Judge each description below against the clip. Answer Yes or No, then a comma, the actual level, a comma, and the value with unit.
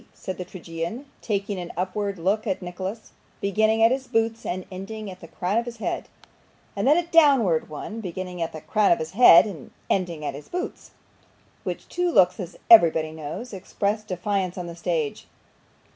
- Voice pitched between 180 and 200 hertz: Yes, high, 190 Hz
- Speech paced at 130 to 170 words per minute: No, average, 185 wpm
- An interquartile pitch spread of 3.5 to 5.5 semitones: Yes, average, 4.2 semitones